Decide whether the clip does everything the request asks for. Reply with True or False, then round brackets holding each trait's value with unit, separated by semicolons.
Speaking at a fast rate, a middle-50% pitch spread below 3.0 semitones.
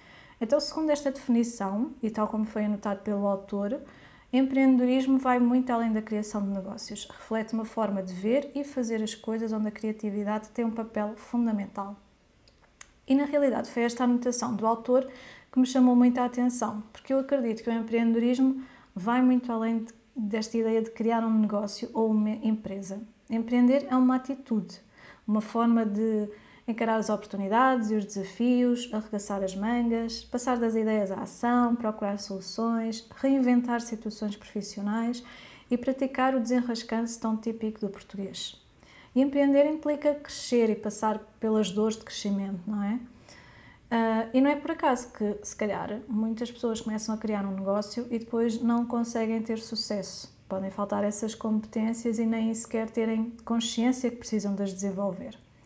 False (160 wpm; 2.4 semitones)